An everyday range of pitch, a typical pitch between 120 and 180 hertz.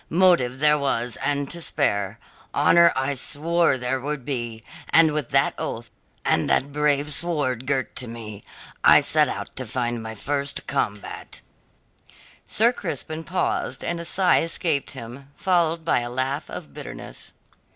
Yes: average, 4.8 semitones; medium, 140 Hz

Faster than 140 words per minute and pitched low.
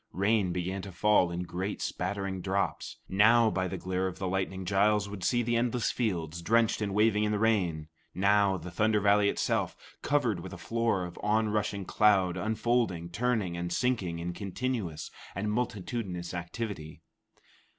Yes: average, 160 wpm; low, 100 Hz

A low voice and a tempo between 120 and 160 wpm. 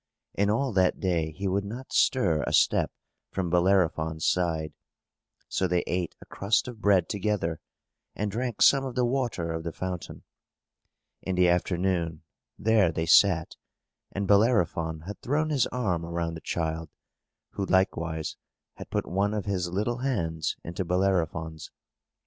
Yes: very low, 90 Hz; average, 150 wpm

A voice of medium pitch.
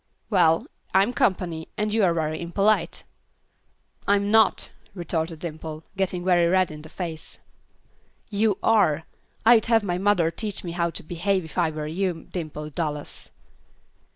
Yes: medium, 175 Hz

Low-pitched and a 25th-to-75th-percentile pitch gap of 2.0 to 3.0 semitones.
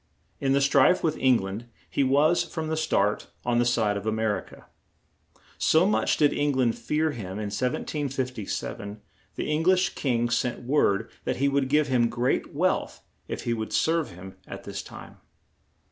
No: low, 130 Hz; average, 5.2 semitones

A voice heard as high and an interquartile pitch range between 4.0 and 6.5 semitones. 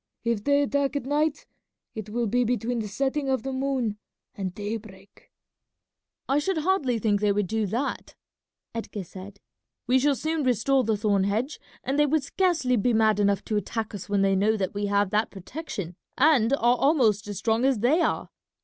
Yes: high, 230 Hz; average, 4.9 semitones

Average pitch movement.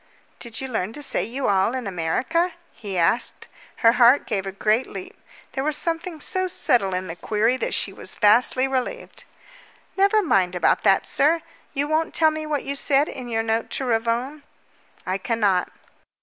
No: wide, 6.3 semitones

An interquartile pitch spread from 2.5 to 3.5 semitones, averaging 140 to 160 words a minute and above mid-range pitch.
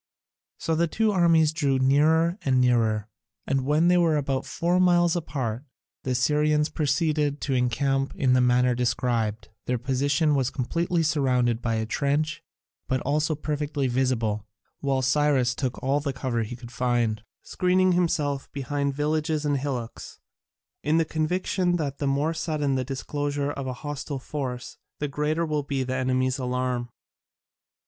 No: average, 3.2 semitones; average, 155 wpm; medium, 140 Hz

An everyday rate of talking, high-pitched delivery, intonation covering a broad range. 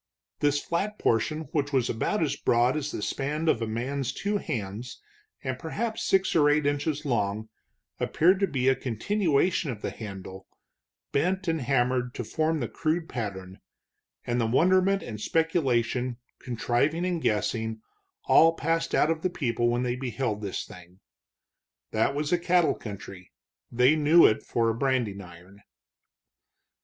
No: average, 155 wpm; low, 135 Hz; wide, 6.0 semitones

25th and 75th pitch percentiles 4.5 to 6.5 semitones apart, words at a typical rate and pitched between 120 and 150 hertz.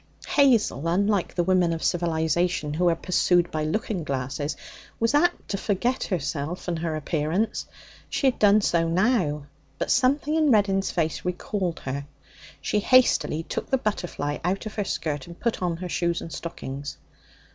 No: average, 4.8 semitones; average, 165 wpm; medium, 175 Hz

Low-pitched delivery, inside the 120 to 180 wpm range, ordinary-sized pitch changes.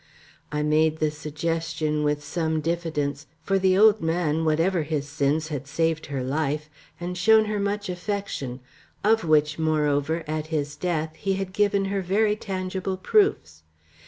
No: medium, 160 Hz; average, 155 wpm; average, 3.9 semitones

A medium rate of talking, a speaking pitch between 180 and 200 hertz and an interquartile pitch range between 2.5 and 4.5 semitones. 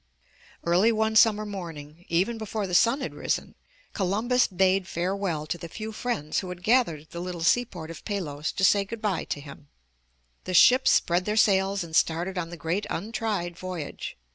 Yes: average, 185 wpm; medium, 185 Hz; average, 4.1 semitones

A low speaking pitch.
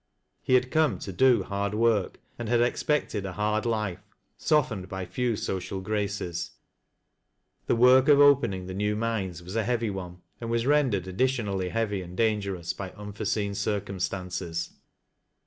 Yes: low, 105 Hz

